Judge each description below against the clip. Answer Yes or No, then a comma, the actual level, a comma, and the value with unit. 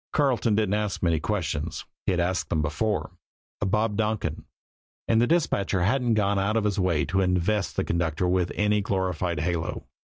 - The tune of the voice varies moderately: Yes, average, 3.4 semitones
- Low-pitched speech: Yes, very low, 95 Hz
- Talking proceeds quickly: No, average, 175 wpm